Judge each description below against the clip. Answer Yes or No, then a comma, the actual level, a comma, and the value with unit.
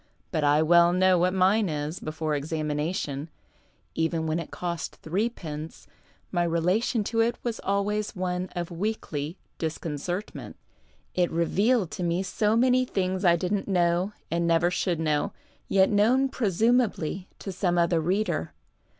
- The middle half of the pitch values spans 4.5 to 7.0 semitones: No, average, 3.7 semitones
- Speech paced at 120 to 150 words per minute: Yes, average, 145 wpm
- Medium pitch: Yes, medium, 180 Hz